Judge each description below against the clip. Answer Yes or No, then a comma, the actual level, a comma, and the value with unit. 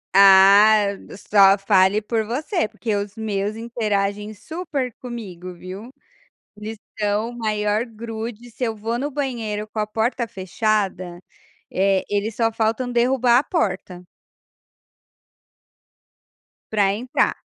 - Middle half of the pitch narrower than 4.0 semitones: Yes, average, 2.8 semitones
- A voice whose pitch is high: Yes, high, 215 Hz